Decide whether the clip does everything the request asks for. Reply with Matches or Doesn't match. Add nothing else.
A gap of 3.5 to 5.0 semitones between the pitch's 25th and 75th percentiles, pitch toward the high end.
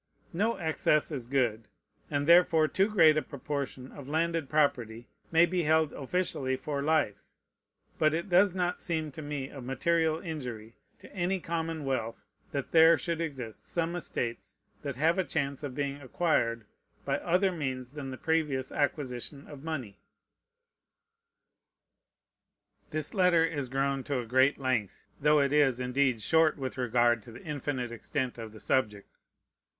Doesn't match